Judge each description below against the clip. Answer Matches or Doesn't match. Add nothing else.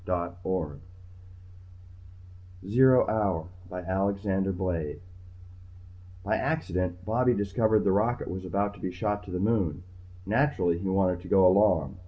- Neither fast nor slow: Doesn't match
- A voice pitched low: Matches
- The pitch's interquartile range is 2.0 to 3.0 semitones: Matches